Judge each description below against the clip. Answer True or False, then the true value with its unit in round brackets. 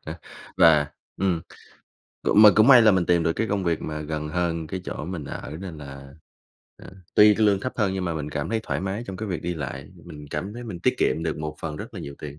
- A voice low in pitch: True (85 Hz)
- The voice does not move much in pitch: False (4.3 semitones)